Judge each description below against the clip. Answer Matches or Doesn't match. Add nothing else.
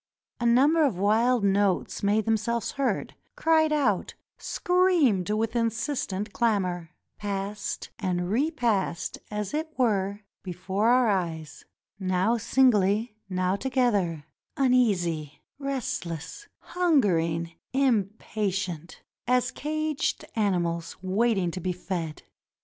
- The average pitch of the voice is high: Matches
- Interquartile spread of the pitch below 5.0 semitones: Doesn't match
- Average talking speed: Doesn't match